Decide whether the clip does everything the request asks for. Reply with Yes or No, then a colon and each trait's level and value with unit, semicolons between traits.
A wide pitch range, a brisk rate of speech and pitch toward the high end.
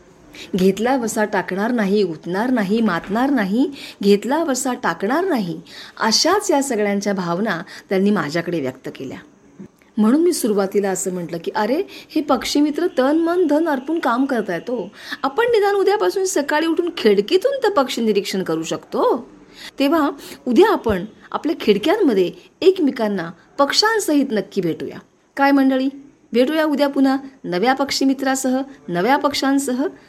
Yes: wide, 7.0 semitones; fast, 135 wpm; very high, 265 Hz